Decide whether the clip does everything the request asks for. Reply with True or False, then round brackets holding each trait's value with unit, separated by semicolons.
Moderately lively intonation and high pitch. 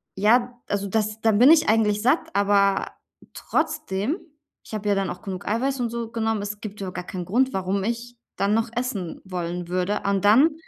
True (3.2 semitones; 210 Hz)